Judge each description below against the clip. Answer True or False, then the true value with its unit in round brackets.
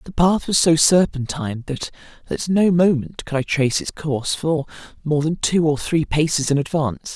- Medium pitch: True (155 Hz)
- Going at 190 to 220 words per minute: True (195 wpm)